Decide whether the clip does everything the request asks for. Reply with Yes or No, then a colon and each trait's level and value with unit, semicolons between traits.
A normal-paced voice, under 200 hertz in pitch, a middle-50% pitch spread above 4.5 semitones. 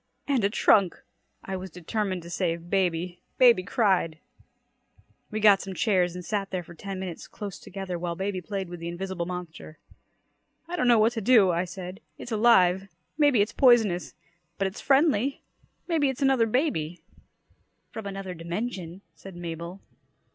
No: average, 160 wpm; high, 190 Hz; average, 3.9 semitones